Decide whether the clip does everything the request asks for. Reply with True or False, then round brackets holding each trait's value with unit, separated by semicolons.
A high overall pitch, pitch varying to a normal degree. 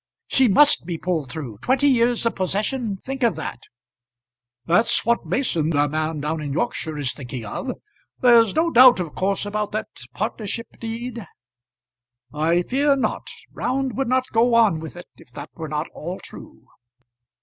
False (205 Hz; 7.4 semitones)